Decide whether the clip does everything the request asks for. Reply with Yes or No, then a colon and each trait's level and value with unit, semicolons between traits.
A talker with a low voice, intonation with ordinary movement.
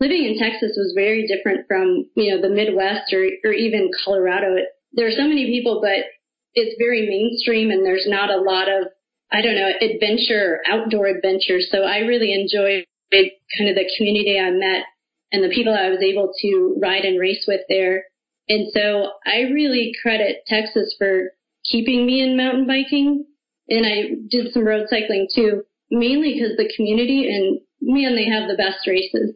No: high, 215 Hz; average, 3.7 semitones